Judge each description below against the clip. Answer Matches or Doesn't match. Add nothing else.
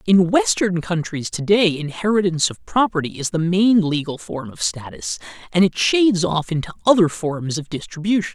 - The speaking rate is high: Doesn't match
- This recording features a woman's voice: Doesn't match